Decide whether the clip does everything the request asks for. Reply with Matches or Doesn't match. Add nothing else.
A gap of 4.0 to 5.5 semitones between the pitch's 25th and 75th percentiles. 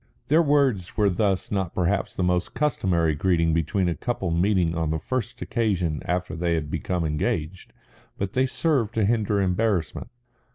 Matches